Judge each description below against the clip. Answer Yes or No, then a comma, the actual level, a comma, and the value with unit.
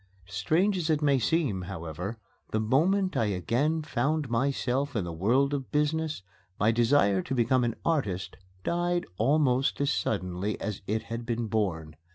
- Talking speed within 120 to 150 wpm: No, average, 160 wpm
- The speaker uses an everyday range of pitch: No, wide, 6.5 semitones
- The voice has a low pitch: Yes, low, 120 Hz